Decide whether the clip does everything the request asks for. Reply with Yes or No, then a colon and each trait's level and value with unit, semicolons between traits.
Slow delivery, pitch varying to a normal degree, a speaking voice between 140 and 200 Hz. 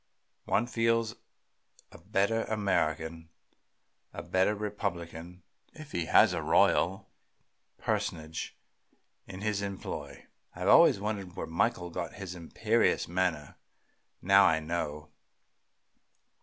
No: slow, 105 wpm; average, 3.8 semitones; very low, 95 Hz